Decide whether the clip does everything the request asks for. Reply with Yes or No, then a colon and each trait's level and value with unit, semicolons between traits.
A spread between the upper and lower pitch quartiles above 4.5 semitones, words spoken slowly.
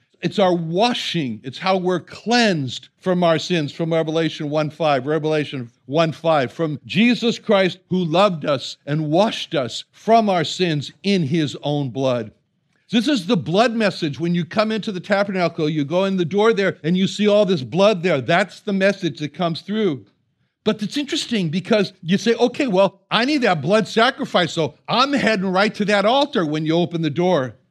No: average, 4.9 semitones; average, 190 wpm